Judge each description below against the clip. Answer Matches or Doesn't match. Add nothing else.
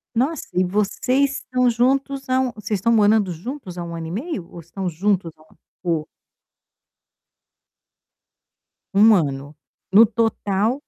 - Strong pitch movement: Matches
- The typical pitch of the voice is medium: Doesn't match